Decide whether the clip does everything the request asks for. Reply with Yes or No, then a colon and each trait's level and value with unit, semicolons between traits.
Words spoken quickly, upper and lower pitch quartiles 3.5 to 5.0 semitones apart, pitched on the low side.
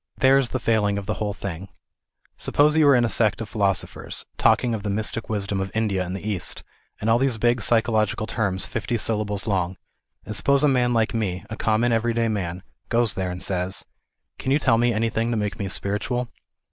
No: fast, 220 wpm; average, 3.1 semitones; low, 110 Hz